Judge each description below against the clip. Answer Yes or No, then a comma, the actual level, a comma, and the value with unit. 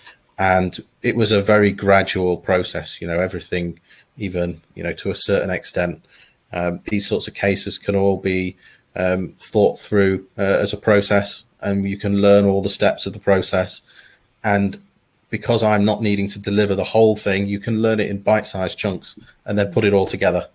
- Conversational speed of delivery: Yes, average, 195 wpm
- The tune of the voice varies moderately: No, narrow, 1.7 semitones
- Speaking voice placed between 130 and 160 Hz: No, low, 100 Hz